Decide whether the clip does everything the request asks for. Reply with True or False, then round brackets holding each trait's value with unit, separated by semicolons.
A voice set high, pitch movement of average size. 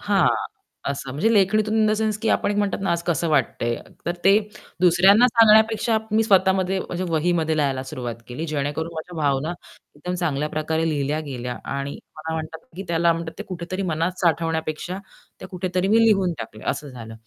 False (170 Hz; 4.1 semitones)